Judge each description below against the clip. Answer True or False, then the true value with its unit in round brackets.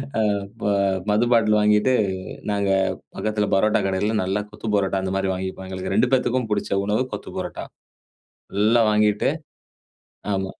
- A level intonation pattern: True (1.9 semitones)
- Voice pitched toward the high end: False (105 Hz)